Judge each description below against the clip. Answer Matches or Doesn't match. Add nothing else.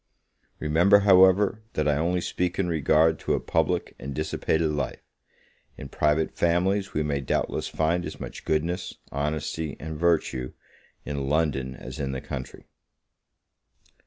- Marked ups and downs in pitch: Doesn't match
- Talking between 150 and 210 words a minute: Doesn't match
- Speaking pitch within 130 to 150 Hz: Doesn't match